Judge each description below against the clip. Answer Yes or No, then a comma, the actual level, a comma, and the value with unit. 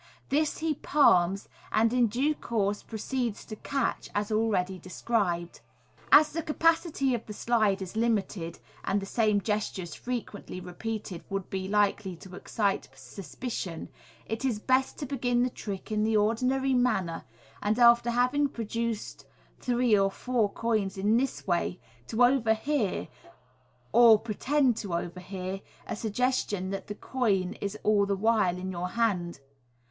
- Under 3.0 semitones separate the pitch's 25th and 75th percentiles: No, average, 4.0 semitones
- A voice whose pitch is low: No, high, 215 Hz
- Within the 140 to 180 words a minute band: Yes, average, 150 wpm